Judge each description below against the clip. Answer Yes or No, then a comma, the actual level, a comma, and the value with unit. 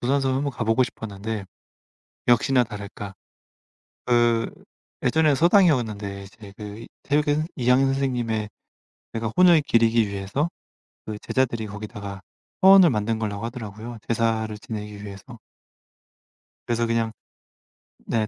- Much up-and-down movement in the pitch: No, average, 3.7 semitones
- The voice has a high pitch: No, low, 115 Hz